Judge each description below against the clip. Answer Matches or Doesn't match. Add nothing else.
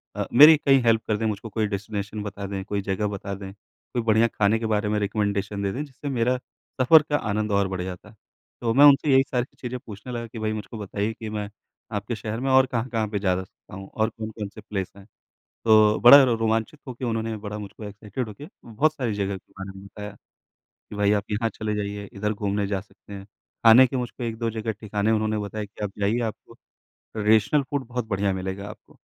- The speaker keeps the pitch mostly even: Matches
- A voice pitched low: Matches